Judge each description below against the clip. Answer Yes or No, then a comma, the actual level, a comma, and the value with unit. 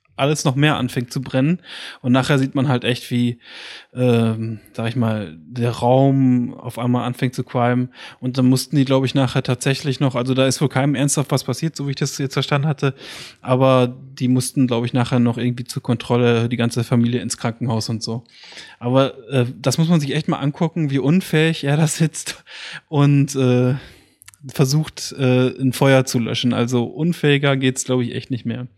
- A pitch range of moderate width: No, narrow, 2.3 semitones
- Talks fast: Yes, fast, 200 wpm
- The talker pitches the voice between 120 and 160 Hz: Yes, low, 130 Hz